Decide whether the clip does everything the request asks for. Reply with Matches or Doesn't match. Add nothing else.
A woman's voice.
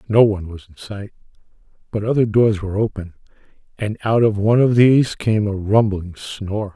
Doesn't match